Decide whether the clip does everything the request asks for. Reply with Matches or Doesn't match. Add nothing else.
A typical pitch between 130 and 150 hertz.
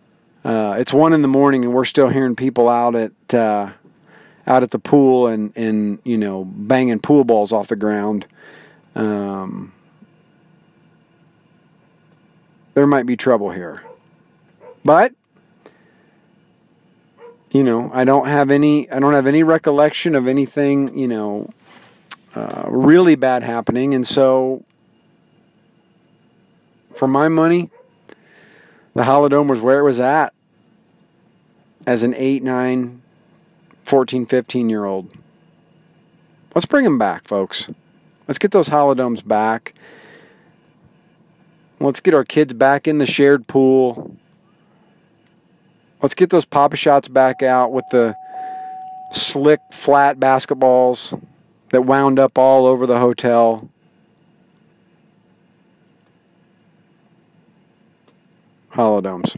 Matches